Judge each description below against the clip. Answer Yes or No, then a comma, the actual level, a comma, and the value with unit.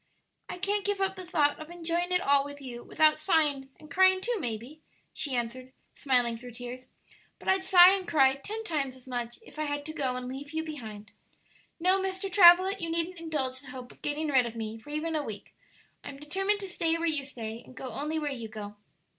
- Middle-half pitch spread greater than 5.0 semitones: Yes, wide, 5.5 semitones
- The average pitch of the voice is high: Yes, very high, 295 Hz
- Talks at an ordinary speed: No, fast, 220 wpm